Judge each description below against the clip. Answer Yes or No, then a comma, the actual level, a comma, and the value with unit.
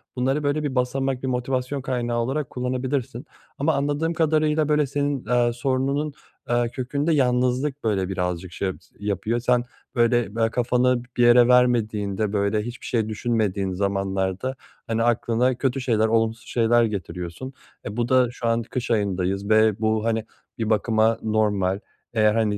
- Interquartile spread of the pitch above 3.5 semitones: No, average, 3.2 semitones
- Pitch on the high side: No, low, 120 Hz